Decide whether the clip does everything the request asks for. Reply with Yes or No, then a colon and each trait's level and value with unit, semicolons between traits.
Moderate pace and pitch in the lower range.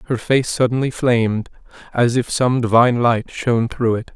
Yes: average, 175 wpm; low, 120 Hz